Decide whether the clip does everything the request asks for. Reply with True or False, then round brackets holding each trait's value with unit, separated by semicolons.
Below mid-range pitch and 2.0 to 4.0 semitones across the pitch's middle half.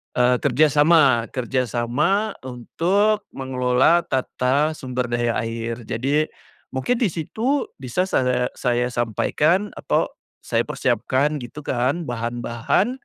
False (130 Hz; 4.7 semitones)